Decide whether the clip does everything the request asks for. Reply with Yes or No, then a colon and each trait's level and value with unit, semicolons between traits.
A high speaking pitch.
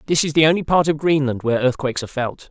No: medium, 145 Hz